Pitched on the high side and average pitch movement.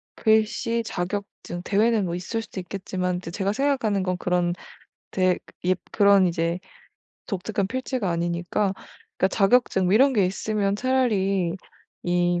Yes: high, 195 Hz; average, 3.4 semitones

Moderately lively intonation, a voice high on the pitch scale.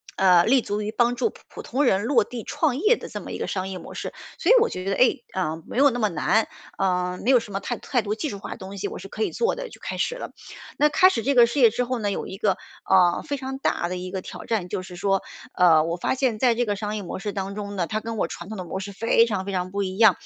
Yes: average, 4.5 semitones; high, 210 Hz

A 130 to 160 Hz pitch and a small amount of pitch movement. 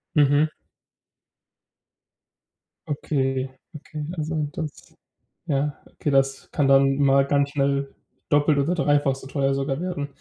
Yes: medium, 140 Hz; narrow, 1.5 semitones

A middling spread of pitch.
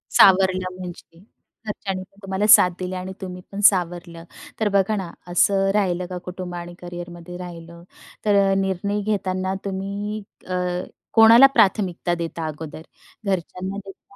No: narrow, 2.0 semitones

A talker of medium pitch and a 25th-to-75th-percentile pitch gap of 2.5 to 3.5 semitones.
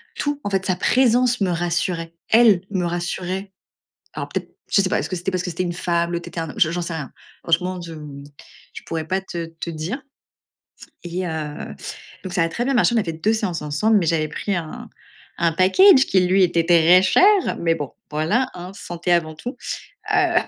Yes: medium, 175 Hz; average, 2.9 semitones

